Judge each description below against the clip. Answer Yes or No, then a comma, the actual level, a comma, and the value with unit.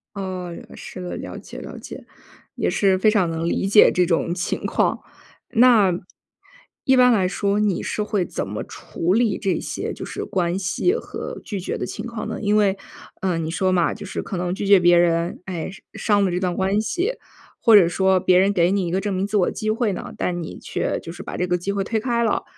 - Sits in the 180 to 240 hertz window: Yes, high, 190 Hz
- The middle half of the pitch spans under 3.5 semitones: Yes, average, 2.9 semitones